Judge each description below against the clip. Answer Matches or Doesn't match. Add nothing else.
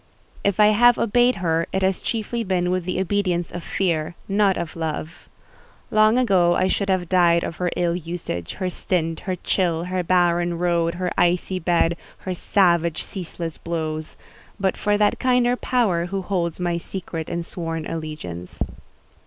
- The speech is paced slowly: Doesn't match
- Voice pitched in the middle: Matches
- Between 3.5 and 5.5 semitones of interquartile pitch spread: Doesn't match